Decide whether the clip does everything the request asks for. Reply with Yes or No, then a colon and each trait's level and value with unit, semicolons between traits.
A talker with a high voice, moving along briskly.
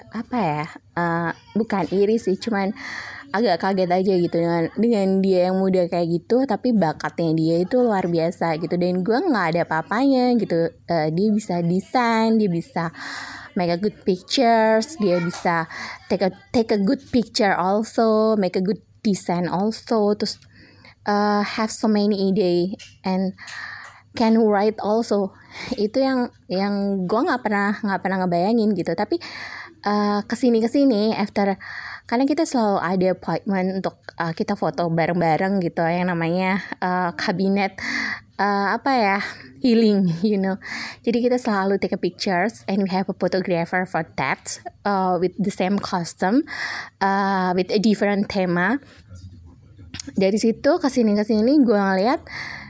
Yes: high, 195 Hz; fast, 150 wpm